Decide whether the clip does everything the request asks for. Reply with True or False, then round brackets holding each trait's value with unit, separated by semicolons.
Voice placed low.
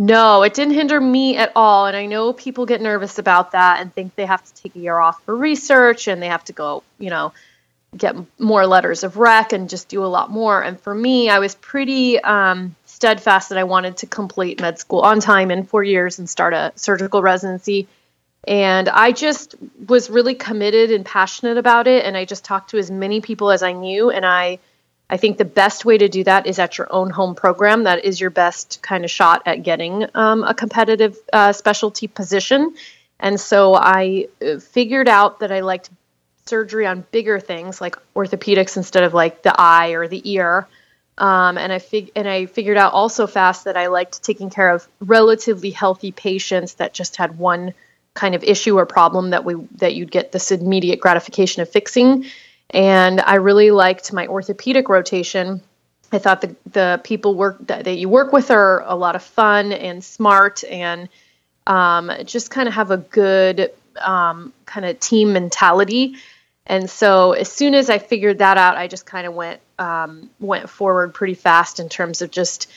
False (195 Hz)